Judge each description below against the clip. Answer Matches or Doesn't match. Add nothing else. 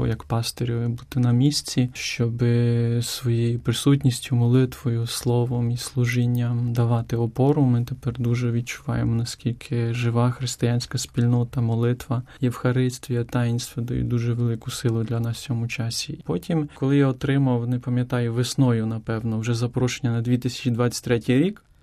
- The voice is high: Doesn't match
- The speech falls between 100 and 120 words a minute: Doesn't match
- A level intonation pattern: Matches